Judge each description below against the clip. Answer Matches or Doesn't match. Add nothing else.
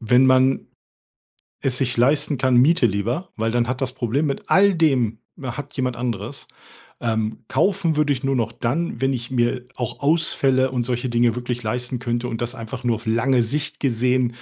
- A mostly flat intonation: Matches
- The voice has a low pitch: Matches